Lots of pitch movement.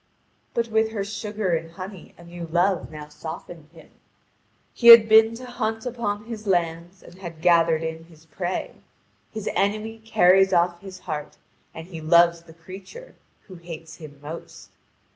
No: average, 4.4 semitones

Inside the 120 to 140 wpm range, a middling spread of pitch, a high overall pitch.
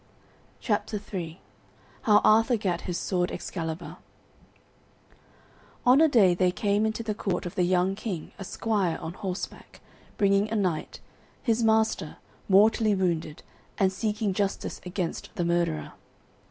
Yes: slow, 135 wpm; average, 3.5 semitones; high, 195 Hz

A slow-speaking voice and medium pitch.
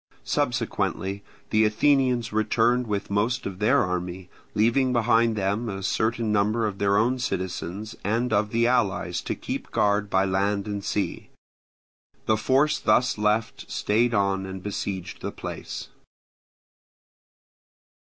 No: slow, 130 wpm; low, 105 Hz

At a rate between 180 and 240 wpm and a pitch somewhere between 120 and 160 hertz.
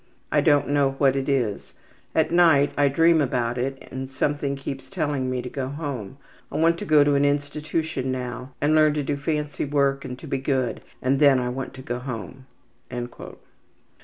Yes: average, 190 wpm; medium, 140 Hz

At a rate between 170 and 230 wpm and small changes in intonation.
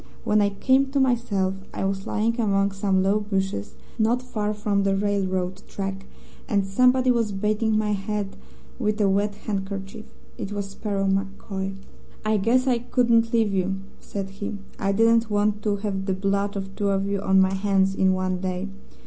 Yes: average, 180 wpm; narrow, 1.7 semitones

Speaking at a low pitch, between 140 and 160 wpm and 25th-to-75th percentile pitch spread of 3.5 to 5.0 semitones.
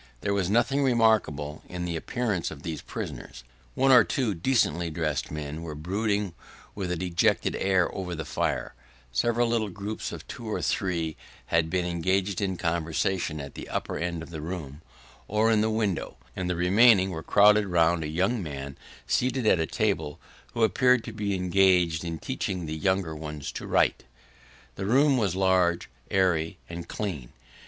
No: very low, 90 Hz; average, 175 wpm; average, 4.4 semitones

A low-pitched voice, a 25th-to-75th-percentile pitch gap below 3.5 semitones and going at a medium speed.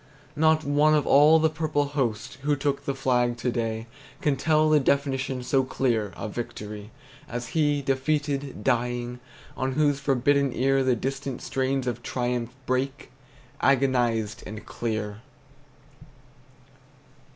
No: low, 130 Hz; average, 2.9 semitones; slow, 130 wpm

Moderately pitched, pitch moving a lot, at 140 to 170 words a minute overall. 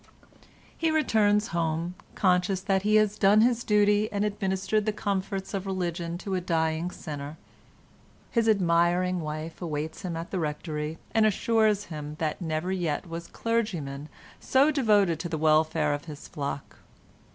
No: medium, 180 Hz; average, 4.6 semitones; average, 150 wpm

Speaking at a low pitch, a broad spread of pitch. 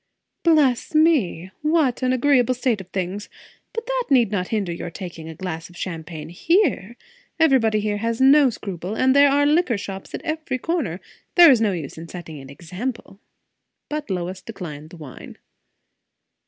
No: high, 215 Hz; wide, 8.0 semitones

